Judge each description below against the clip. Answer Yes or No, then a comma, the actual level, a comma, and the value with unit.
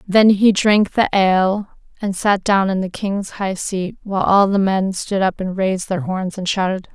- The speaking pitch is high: Yes, high, 195 Hz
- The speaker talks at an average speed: No, fast, 215 wpm